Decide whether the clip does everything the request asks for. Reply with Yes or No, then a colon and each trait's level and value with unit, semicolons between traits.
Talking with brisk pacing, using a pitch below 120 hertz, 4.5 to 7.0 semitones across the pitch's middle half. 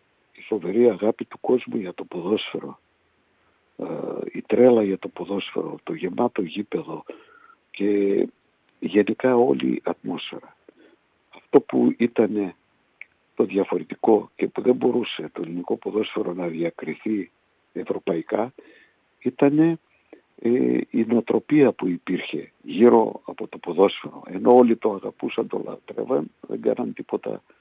No: slow, 115 wpm; low, 110 Hz; average, 4.9 semitones